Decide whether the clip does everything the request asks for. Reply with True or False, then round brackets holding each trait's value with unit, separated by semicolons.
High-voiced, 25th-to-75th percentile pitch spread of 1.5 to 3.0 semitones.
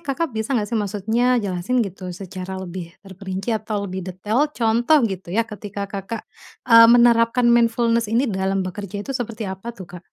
False (210 Hz; 3.4 semitones)